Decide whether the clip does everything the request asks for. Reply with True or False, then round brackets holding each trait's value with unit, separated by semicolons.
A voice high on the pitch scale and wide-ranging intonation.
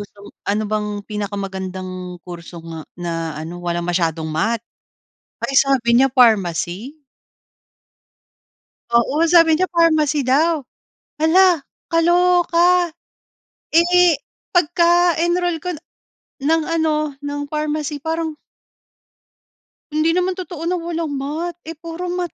True (300 Hz; 8.8 semitones)